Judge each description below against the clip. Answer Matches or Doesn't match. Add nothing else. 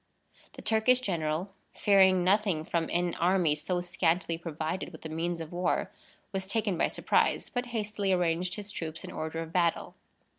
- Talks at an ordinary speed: Matches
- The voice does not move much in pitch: Doesn't match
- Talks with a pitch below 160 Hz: Doesn't match